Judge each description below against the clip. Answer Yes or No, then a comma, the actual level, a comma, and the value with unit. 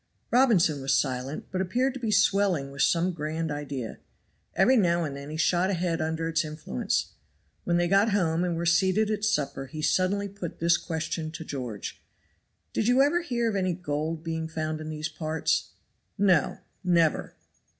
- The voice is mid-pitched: Yes, medium, 165 Hz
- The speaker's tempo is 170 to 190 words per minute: Yes, average, 175 wpm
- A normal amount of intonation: Yes, average, 3.9 semitones